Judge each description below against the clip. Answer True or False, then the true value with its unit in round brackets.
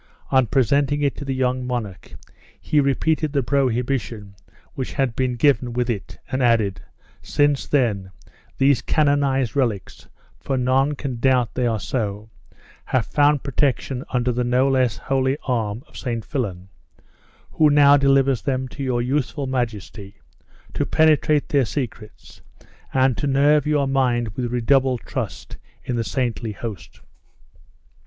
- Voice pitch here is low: True (130 Hz)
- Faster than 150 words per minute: False (145 wpm)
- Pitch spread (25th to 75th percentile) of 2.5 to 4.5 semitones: True (2.9 semitones)